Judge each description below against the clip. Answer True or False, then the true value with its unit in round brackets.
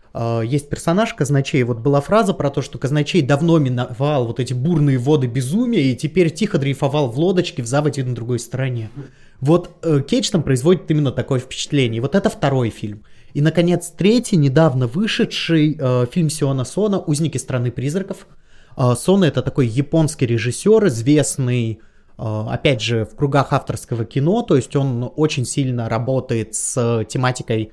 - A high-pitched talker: False (140 Hz)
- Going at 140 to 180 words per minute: True (155 wpm)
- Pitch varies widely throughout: False (4.6 semitones)